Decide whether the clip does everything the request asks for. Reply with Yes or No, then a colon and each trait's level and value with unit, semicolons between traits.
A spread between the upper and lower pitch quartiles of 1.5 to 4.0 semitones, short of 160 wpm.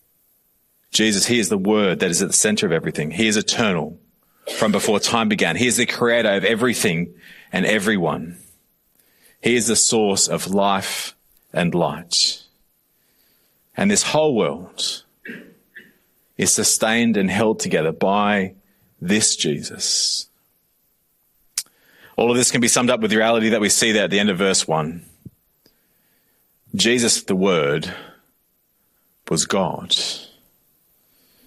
Yes: average, 2.9 semitones; slow, 135 wpm